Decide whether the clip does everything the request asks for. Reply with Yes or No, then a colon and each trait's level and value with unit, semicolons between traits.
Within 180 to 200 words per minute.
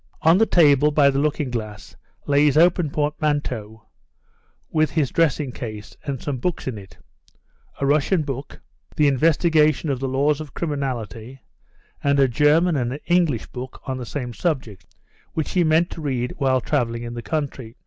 No: average, 170 wpm